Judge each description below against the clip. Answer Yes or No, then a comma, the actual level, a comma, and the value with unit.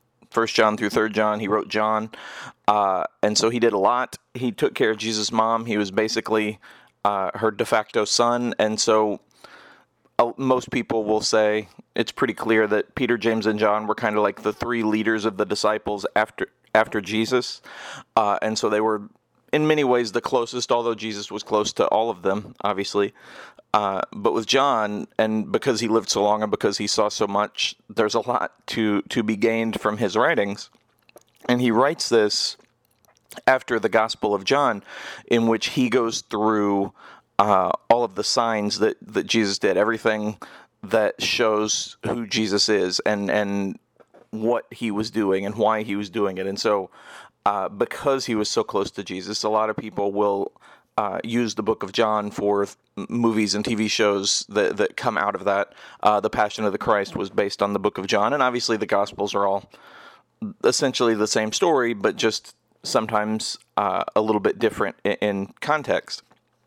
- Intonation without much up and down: Yes, narrow, 1.6 semitones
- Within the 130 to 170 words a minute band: No, average, 190 wpm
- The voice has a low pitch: Yes, low, 110 Hz